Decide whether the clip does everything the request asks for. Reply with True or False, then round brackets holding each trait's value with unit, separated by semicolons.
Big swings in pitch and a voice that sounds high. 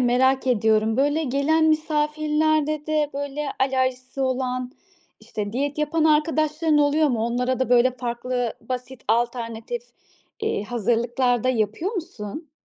False (3.8 semitones; 260 Hz)